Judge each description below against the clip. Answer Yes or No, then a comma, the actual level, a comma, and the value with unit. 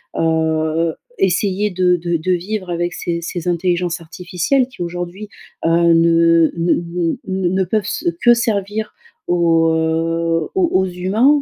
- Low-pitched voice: No, medium, 175 Hz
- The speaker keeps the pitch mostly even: Yes, narrow, 2.3 semitones